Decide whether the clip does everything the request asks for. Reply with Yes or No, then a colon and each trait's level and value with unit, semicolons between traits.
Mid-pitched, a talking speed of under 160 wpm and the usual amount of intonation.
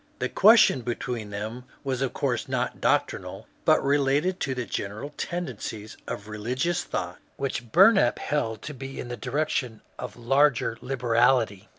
No: low, 125 Hz; average, 150 wpm; average, 4.0 semitones